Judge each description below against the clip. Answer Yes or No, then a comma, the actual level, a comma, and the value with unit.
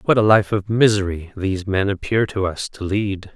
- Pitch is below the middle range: Yes, low, 100 Hz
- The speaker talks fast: Yes, fast, 215 wpm